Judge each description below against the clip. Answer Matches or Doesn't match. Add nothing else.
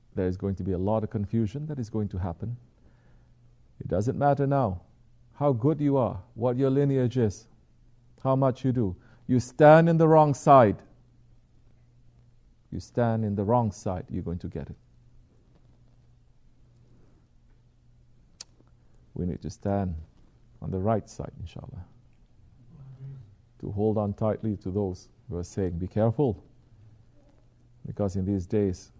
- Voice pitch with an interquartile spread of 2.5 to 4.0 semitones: Matches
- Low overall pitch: Matches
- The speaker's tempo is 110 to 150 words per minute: Matches